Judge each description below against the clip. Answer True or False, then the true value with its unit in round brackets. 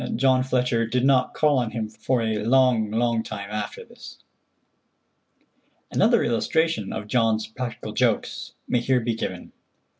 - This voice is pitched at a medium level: False (115 Hz)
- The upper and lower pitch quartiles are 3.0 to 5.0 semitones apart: False (2.6 semitones)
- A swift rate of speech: False (145 wpm)